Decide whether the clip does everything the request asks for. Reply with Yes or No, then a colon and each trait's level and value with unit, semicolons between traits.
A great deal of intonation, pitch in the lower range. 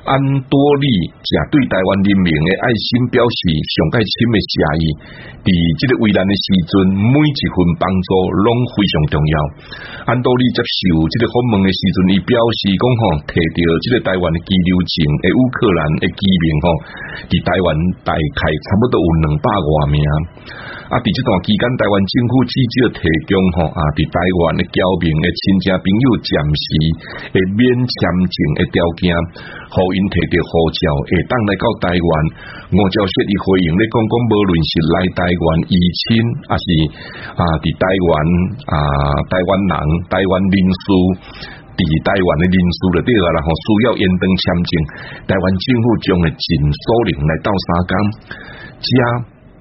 No: average, 4.4 semitones; very low, 95 Hz